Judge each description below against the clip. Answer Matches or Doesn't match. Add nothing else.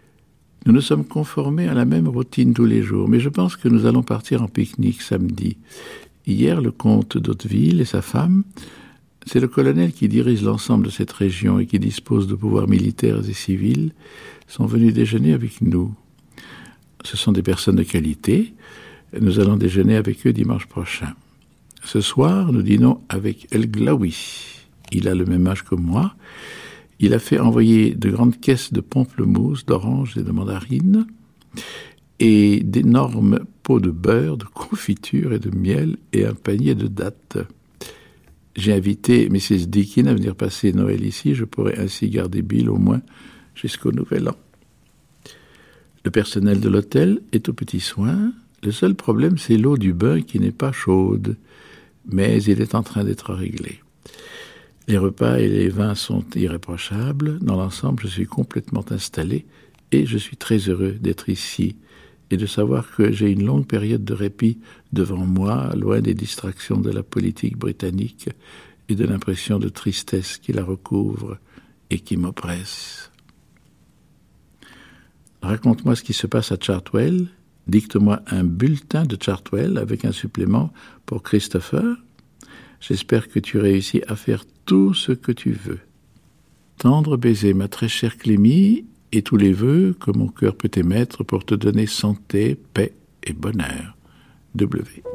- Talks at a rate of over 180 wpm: Doesn't match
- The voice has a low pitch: Matches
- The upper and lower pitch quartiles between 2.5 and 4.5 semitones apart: Matches